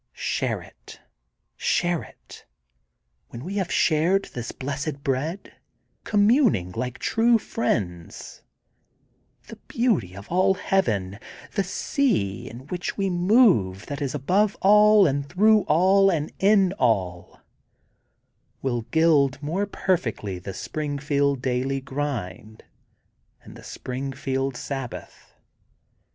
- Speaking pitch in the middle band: Yes, medium, 145 Hz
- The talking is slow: Yes, slow, 110 wpm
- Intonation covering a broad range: Yes, wide, 7.5 semitones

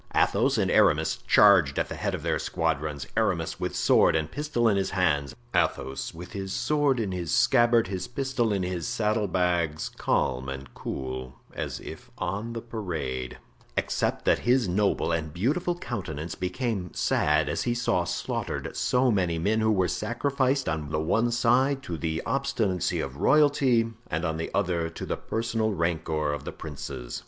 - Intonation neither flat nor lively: No, wide, 6.6 semitones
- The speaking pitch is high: No, very low, 95 Hz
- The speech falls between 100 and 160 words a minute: No, average, 170 wpm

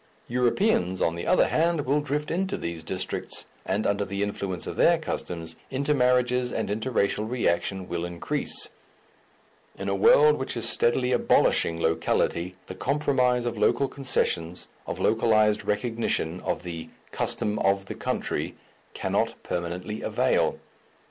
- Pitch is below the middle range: Yes, low, 110 Hz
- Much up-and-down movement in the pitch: Yes, wide, 5.8 semitones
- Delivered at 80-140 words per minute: Yes, slow, 135 wpm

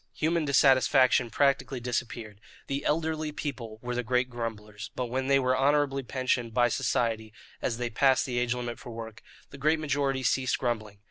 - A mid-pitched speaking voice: No, low, 125 Hz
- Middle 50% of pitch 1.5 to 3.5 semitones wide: Yes, narrow, 2.6 semitones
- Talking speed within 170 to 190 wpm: Yes, average, 175 wpm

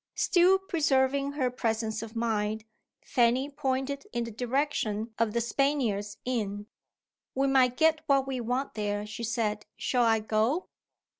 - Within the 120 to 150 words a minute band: Yes, average, 145 wpm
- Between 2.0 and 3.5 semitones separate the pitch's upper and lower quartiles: No, average, 3.9 semitones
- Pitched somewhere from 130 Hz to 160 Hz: No, high, 245 Hz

